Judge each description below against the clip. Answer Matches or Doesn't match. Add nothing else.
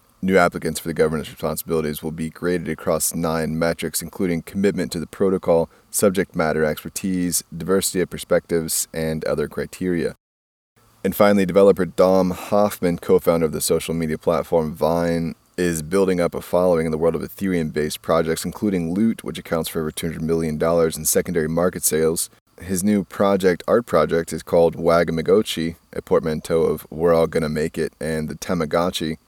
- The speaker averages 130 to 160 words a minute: Doesn't match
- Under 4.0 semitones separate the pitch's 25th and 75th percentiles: Matches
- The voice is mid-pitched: Doesn't match